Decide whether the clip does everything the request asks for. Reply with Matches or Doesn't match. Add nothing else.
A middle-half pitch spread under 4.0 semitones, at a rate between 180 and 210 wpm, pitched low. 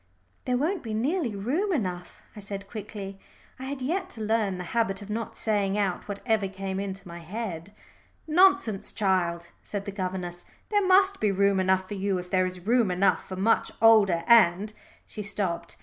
Doesn't match